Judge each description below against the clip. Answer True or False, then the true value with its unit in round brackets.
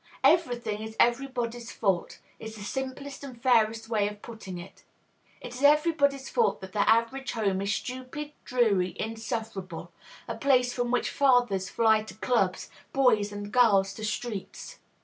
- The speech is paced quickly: False (155 wpm)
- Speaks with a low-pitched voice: False (230 Hz)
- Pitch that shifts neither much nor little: True (3.6 semitones)